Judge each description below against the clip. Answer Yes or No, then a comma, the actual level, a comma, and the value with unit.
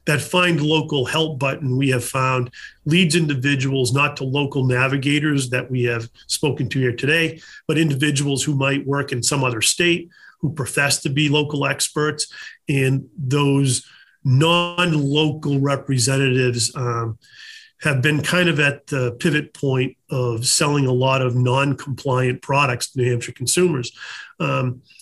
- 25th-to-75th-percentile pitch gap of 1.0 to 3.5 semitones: Yes, average, 2.8 semitones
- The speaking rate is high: No, average, 150 wpm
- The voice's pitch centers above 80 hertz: Yes, medium, 140 Hz